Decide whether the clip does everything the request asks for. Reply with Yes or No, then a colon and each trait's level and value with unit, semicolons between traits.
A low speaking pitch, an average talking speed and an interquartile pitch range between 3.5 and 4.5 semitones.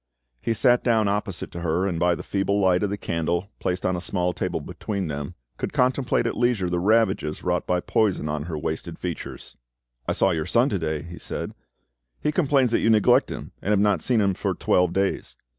No: very low, 95 Hz; fast, 215 wpm; average, 3.8 semitones